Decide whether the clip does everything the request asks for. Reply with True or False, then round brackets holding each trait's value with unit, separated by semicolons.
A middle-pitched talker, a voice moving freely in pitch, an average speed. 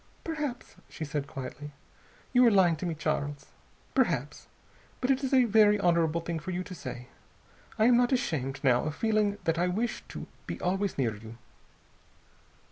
True (175 Hz; 7.0 semitones; 175 wpm)